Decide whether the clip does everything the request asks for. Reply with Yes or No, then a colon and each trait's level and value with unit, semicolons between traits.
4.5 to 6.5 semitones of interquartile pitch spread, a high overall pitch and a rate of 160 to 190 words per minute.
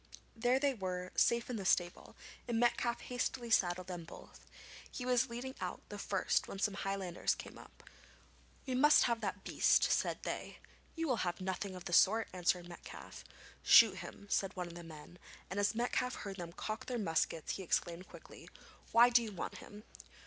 Yes: average, 4.9 semitones; high, 200 Hz; average, 185 wpm